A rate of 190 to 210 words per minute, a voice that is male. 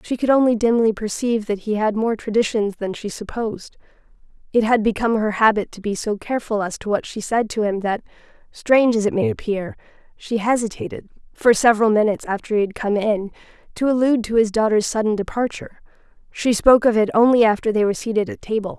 No: average, 200 wpm; female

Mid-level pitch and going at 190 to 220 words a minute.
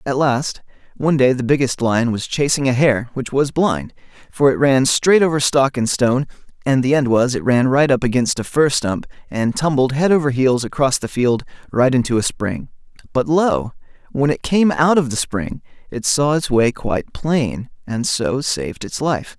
No: low, 130 Hz; fast, 205 wpm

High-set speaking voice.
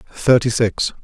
No: low, 115 Hz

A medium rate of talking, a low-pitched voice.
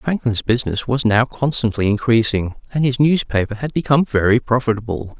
Yes: average, 150 wpm; low, 120 Hz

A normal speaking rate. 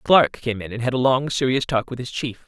No: fast, 290 wpm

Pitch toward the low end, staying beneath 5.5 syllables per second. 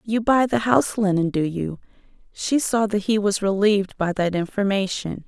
No: high, 200 Hz; 5.0 syllables/s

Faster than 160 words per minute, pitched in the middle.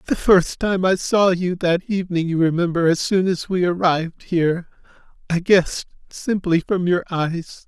Yes: average, 170 wpm; medium, 175 Hz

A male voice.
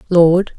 No: female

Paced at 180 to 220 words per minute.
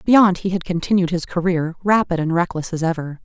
Yes: fast, 205 wpm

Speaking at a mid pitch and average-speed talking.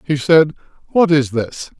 Yes: medium, 150 Hz; average, 165 wpm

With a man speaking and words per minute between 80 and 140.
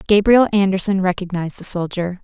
No: female; slow, 135 wpm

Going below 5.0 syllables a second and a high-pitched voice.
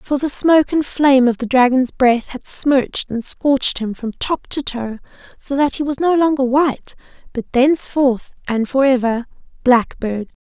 Yes: 4.6 syllables/s; very high, 265 Hz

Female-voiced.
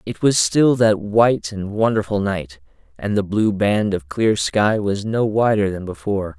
No: male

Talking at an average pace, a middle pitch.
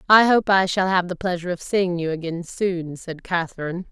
No: fast, 215 wpm; medium, 180 Hz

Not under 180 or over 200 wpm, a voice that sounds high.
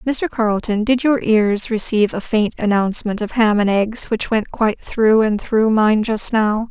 Yes: average, 195 wpm; high, 220 Hz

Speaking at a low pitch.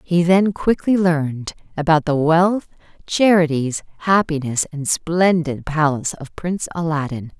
No: medium, 165 Hz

